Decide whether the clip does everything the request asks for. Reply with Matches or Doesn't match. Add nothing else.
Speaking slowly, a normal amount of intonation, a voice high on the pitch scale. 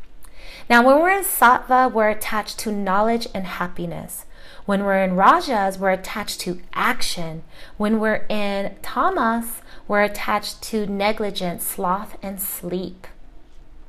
Matches